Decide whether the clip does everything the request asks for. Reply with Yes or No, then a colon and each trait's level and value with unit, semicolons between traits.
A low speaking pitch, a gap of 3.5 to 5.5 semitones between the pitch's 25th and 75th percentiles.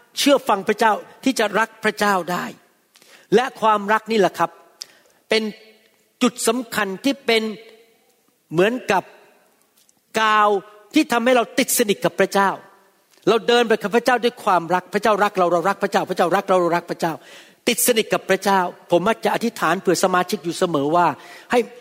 No: high, 210 Hz; average, 3.8 semitones